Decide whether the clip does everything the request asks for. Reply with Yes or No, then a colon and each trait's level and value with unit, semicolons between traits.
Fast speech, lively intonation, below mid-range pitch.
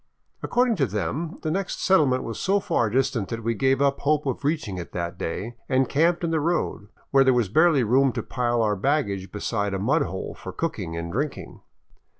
Yes: fast, 210 wpm; wide, 6.5 semitones; low, 130 Hz